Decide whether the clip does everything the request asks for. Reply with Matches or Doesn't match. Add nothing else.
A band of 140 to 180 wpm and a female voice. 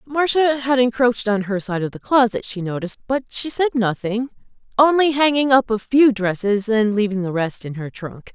Doesn't match